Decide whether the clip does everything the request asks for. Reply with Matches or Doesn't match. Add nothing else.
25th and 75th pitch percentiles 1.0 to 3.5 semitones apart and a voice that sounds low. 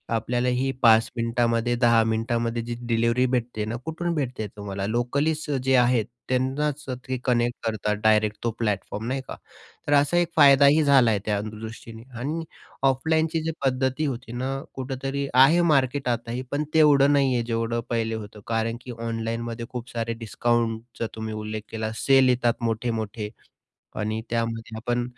Matches